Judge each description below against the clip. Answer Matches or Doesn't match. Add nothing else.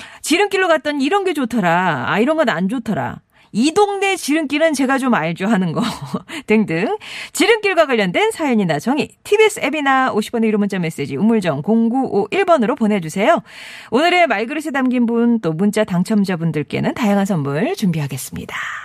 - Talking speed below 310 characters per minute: Doesn't match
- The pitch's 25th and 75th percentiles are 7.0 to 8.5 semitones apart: Matches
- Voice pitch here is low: Doesn't match